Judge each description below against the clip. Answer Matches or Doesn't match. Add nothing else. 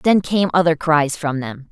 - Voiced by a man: Doesn't match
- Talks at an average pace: Doesn't match